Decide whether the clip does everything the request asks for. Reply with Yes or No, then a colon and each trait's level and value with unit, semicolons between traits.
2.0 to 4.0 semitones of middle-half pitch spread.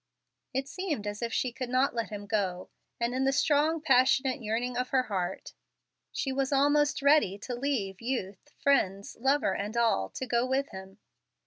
No: average, 4.8 semitones